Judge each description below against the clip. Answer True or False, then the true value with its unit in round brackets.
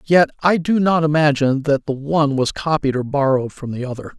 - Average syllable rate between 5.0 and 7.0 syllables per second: True (5.9 syllables/s)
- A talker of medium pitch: True (145 Hz)